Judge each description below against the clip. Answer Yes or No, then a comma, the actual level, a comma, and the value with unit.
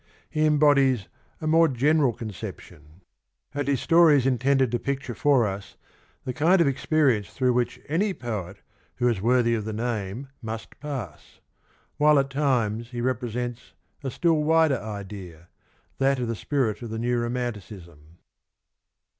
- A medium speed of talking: Yes, average, 155 wpm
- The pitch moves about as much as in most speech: Yes, average, 4.3 semitones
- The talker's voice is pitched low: Yes, low, 125 Hz